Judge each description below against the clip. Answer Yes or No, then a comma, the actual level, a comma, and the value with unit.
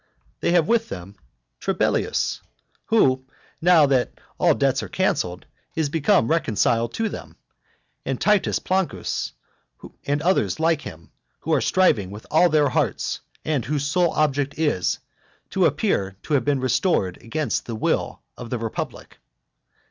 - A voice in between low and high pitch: Yes, medium, 145 Hz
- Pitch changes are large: Yes, wide, 6.3 semitones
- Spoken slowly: No, average, 145 wpm